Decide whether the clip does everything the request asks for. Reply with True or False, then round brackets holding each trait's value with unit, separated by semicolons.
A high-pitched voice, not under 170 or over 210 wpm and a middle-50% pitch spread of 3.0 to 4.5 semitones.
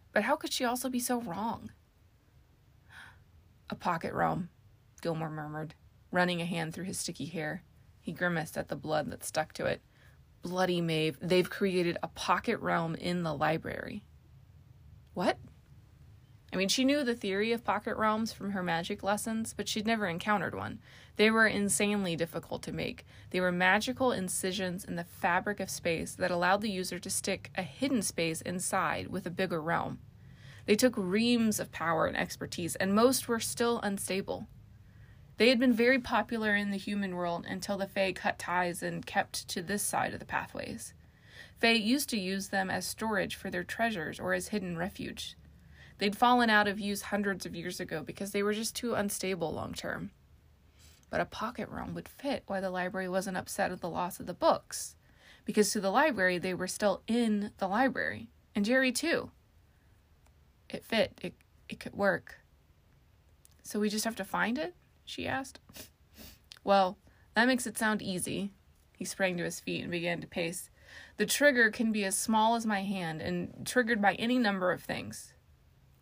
True (195 Hz; 180 wpm; 4.1 semitones)